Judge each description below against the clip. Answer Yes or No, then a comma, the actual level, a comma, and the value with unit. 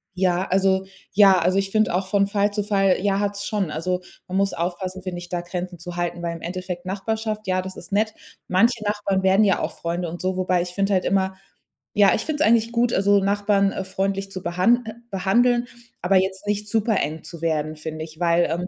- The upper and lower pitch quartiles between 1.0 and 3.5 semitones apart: Yes, narrow, 2.4 semitones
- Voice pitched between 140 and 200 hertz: Yes, high, 190 Hz